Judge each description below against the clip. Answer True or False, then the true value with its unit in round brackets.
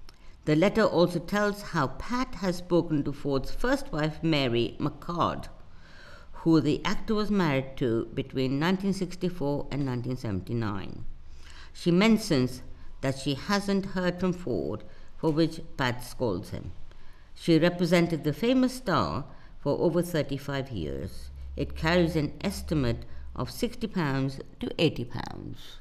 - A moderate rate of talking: False (130 wpm)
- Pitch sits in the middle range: True (150 Hz)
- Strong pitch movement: True (6.8 semitones)